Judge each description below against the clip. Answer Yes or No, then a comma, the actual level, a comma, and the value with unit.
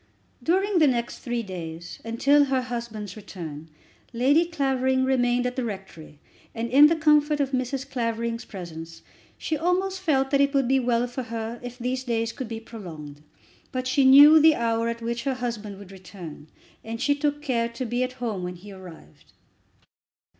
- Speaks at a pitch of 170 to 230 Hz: No, high, 240 Hz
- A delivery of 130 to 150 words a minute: No, average, 180 wpm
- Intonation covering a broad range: No, average, 3.9 semitones